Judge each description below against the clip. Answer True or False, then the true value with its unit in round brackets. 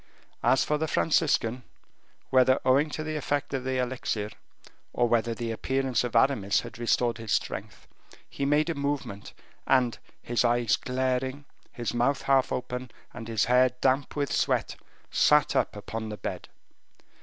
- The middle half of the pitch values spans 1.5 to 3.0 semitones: True (2.7 semitones)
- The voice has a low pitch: True (125 Hz)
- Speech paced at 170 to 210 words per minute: False (155 wpm)